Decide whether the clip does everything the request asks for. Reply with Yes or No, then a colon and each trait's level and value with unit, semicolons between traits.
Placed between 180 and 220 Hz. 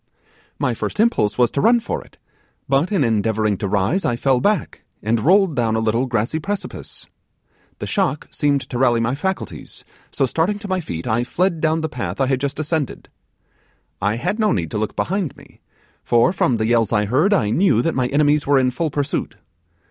No: low, 135 Hz